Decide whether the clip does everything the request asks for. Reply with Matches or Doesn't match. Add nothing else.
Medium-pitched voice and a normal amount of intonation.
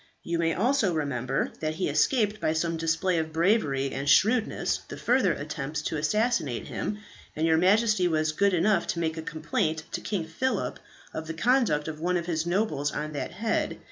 Matches